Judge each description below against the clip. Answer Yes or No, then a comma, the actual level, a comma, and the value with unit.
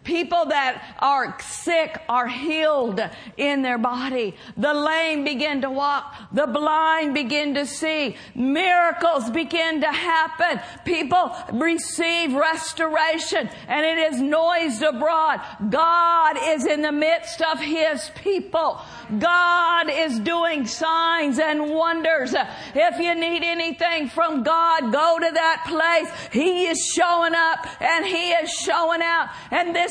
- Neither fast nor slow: No, slow, 130 wpm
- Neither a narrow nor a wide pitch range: No, narrow, 2.2 semitones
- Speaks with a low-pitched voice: No, very high, 320 Hz